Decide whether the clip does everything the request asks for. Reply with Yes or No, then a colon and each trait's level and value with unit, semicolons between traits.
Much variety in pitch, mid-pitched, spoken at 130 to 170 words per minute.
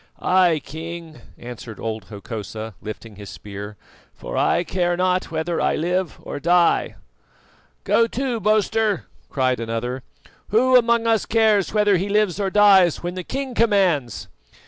Yes: wide, 9.0 semitones; medium, 175 Hz; average, 145 wpm